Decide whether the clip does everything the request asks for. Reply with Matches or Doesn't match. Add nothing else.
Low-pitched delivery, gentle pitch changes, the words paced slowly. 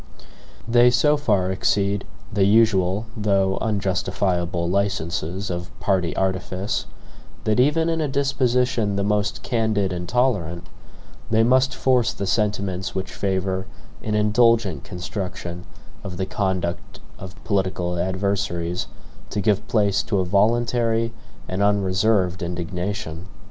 Doesn't match